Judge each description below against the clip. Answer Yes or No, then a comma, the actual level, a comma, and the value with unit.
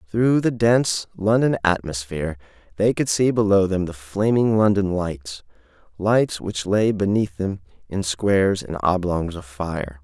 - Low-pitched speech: Yes, low, 100 Hz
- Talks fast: No, average, 150 wpm